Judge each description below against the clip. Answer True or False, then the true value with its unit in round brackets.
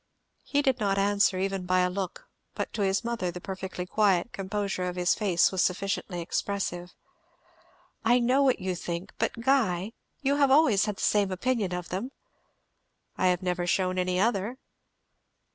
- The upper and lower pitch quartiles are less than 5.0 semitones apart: True (3.6 semitones)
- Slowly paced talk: False (165 wpm)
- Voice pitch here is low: False (195 Hz)